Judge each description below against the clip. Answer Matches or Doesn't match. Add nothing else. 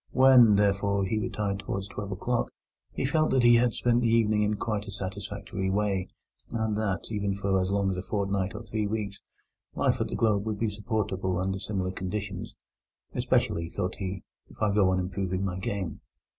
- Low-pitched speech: Matches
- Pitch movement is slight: Matches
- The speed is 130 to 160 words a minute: Doesn't match